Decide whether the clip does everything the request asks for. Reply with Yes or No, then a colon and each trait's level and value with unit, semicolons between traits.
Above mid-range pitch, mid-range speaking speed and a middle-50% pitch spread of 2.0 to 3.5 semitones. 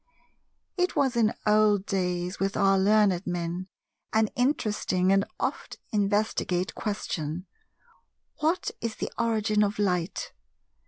No: high, 205 Hz; slow, 115 wpm; average, 2.9 semitones